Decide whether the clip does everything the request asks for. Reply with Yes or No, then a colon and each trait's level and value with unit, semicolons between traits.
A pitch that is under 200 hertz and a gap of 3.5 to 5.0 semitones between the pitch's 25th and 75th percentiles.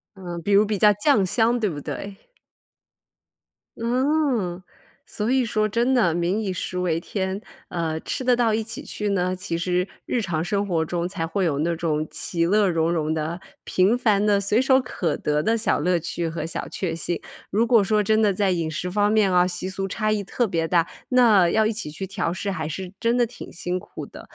Yes: high, 190 Hz; average, 4.0 semitones